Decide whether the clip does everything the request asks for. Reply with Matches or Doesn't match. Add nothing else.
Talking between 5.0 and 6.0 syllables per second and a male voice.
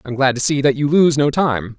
Matches